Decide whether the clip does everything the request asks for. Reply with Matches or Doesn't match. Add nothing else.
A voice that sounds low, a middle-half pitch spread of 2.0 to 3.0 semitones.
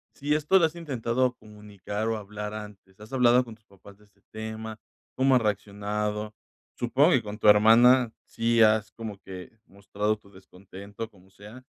Matches